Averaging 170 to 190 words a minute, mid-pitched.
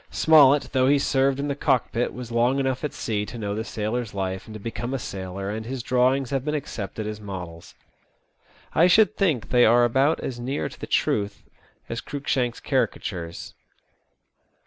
No: average, 180 wpm; low, 120 Hz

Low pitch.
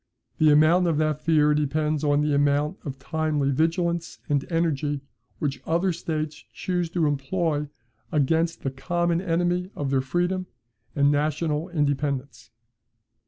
No: medium, 155 Hz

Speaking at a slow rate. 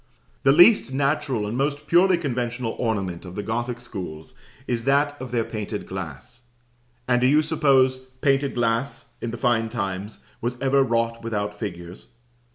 No: average, 160 wpm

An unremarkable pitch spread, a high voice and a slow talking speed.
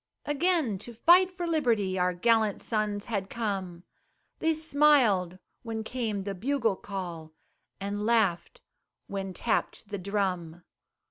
Yes: average, 4.7 semitones; high, 210 Hz; slow, 125 wpm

